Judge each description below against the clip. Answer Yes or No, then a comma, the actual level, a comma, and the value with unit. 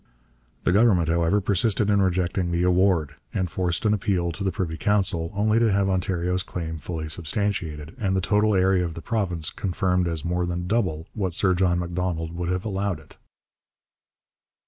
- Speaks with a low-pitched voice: Yes, very low, 90 Hz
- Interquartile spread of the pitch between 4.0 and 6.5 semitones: No, narrow, 2.6 semitones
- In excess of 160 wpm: Yes, average, 175 wpm